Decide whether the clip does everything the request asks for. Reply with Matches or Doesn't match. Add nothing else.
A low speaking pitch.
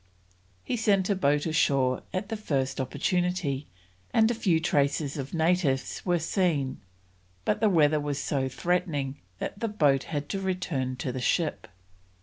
Doesn't match